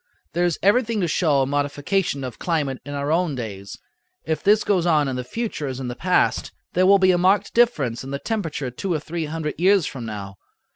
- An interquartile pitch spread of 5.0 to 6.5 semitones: Yes, wide, 5.6 semitones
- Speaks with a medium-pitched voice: Yes, medium, 155 Hz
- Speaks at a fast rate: Yes, fast, 225 wpm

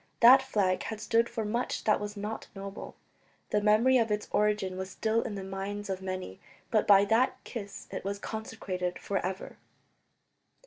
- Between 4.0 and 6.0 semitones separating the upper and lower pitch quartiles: No, narrow, 2.5 semitones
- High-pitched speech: Yes, high, 210 Hz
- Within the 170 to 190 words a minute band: Yes, average, 175 wpm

